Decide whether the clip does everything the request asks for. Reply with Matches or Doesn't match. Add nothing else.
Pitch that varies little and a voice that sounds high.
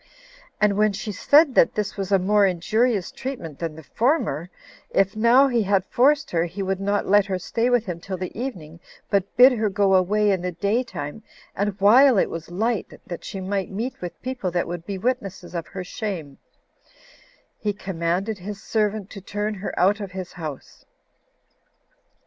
Doesn't match